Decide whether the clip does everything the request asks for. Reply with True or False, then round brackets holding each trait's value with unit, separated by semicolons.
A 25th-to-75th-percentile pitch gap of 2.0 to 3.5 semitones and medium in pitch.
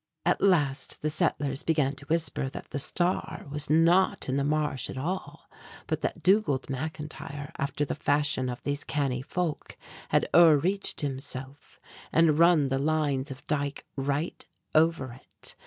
True (2.8 semitones; 145 Hz)